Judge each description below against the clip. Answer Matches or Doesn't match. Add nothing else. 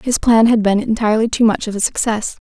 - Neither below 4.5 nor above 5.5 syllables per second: Doesn't match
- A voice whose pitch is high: Matches